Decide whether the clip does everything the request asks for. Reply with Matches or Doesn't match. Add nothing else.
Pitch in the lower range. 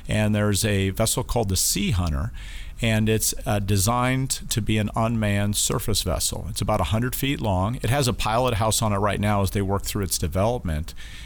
Matches